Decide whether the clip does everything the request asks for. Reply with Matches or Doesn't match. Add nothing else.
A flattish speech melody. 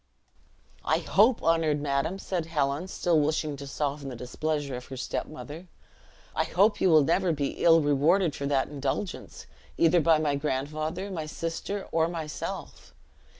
Doesn't match